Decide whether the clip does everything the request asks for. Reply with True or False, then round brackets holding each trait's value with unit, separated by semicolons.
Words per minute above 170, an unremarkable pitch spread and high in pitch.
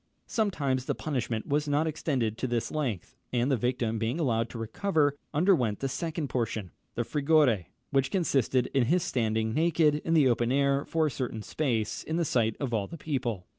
False (190 wpm; 4.9 semitones; 130 Hz)